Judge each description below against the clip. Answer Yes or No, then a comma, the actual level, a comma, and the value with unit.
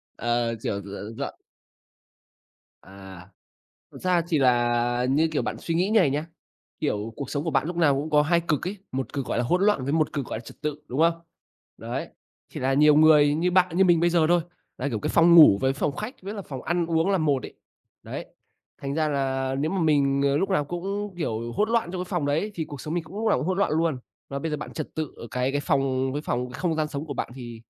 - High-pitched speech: No, medium, 150 Hz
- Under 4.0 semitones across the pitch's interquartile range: No, average, 4.4 semitones